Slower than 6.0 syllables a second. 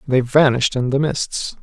Yes: 4.8 syllables/s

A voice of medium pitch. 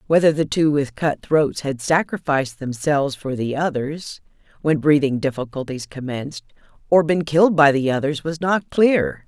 Yes: medium, 150 Hz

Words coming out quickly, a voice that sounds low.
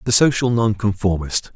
No: slow, 115 wpm; low, 110 Hz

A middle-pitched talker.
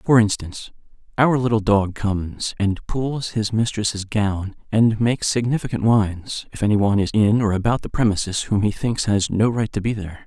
No: low, 110 Hz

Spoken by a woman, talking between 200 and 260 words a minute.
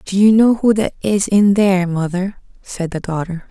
Yes: female; fast, 205 wpm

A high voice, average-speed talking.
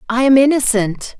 Yes: high, 245 Hz; average, 150 wpm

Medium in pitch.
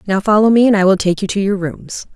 No: high, 200 Hz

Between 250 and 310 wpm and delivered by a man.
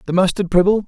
No: fast, 205 wpm; male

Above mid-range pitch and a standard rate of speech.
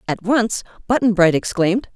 Yes: high, 205 Hz; average, 155 wpm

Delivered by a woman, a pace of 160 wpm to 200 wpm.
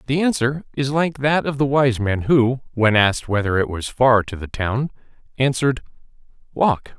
No: male; average, 180 wpm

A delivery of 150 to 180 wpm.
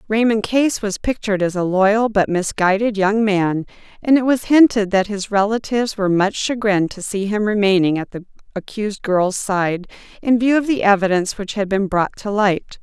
No: average, 190 wpm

